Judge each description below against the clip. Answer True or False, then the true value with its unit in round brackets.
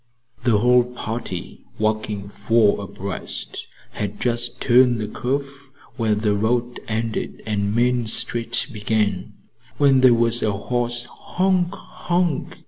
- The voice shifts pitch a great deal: False (2.7 semitones)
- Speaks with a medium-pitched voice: False (115 Hz)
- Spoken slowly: True (125 wpm)